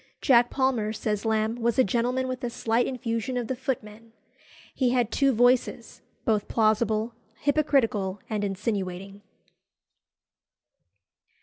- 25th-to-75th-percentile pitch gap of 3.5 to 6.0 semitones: No, average, 2.8 semitones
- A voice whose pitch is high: Yes, high, 230 Hz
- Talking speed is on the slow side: Yes, slow, 120 wpm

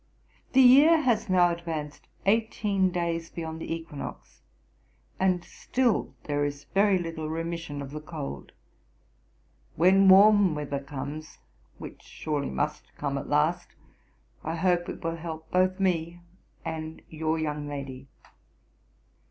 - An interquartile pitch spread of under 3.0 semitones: No, average, 3.7 semitones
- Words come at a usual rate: No, slow, 125 wpm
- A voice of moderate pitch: Yes, medium, 165 Hz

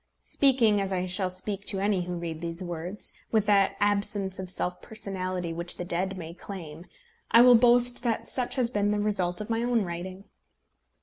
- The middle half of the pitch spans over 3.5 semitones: No, average, 3.0 semitones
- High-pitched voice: Yes, high, 195 Hz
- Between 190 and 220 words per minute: Yes, average, 195 wpm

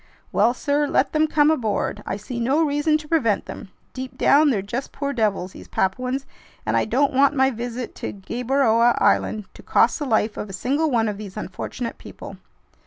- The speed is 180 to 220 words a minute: Yes, average, 195 wpm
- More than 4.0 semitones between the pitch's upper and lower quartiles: Yes, average, 4.7 semitones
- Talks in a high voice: Yes, very high, 250 Hz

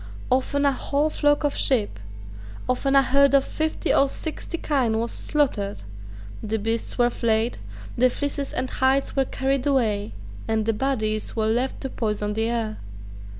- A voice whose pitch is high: Yes, very high, 255 Hz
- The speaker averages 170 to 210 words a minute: No, average, 160 wpm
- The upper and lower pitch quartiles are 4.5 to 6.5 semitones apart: No, average, 3.9 semitones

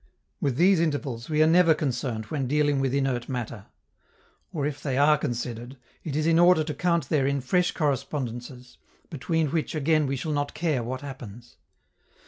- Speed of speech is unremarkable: Yes, average, 170 wpm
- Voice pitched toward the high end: No, medium, 140 Hz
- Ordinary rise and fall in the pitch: Yes, average, 3.6 semitones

